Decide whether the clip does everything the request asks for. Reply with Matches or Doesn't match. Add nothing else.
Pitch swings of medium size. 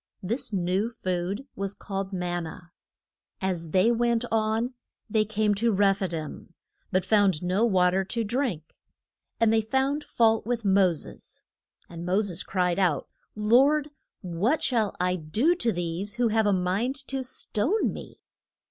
Matches